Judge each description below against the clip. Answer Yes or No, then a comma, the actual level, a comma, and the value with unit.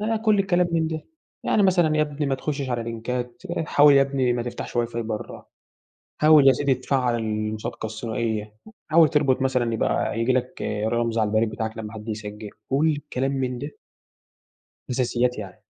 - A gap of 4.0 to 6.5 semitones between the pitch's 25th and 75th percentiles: Yes, average, 4.3 semitones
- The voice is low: Yes, low, 125 Hz